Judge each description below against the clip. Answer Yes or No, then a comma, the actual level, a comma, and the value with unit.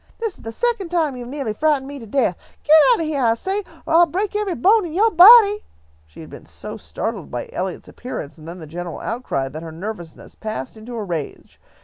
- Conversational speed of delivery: No, fast, 235 wpm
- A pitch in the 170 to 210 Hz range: No, very high, 260 Hz